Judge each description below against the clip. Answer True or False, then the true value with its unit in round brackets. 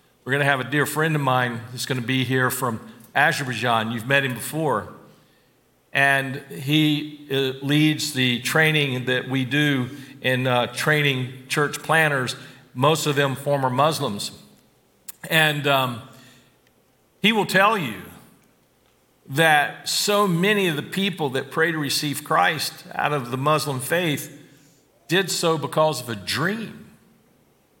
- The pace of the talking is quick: False (145 wpm)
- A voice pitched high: False (140 Hz)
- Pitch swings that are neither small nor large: True (3.2 semitones)